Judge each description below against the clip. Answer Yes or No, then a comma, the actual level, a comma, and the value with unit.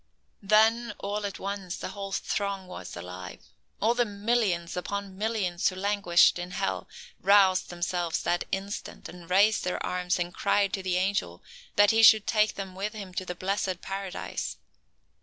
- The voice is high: Yes, high, 195 Hz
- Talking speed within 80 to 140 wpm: No, average, 165 wpm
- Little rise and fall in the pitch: Yes, narrow, 2.3 semitones